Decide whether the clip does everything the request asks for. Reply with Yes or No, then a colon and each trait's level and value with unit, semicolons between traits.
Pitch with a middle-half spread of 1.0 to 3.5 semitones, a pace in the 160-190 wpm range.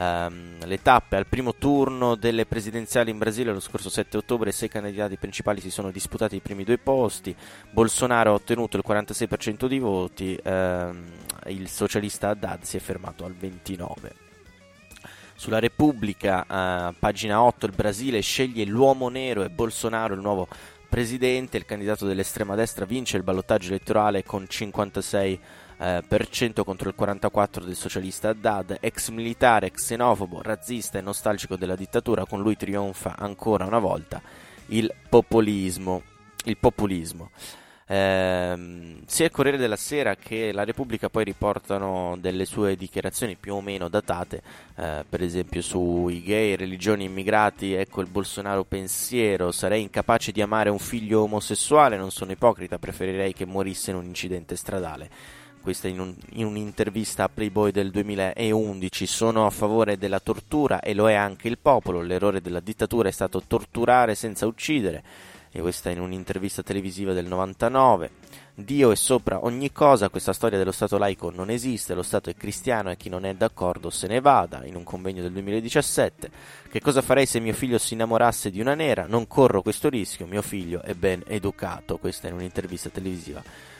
Yes: average, 3.0 semitones; average, 165 wpm